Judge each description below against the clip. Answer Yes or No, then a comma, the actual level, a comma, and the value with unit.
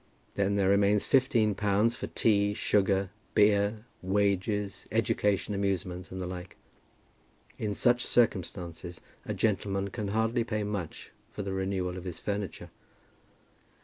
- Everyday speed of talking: No, slow, 130 wpm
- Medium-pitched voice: No, low, 100 Hz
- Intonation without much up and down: Yes, narrow, 1.7 semitones